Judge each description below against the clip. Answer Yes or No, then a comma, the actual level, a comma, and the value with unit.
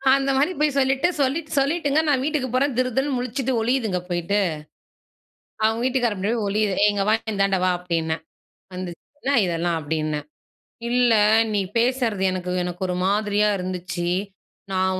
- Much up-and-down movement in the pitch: Yes, wide, 6.3 semitones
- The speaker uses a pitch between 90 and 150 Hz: No, high, 210 Hz